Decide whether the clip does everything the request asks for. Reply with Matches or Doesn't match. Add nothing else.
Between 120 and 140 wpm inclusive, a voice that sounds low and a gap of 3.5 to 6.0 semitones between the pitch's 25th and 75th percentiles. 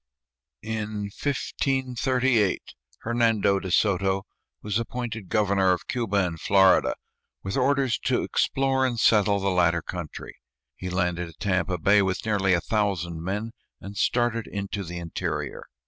Matches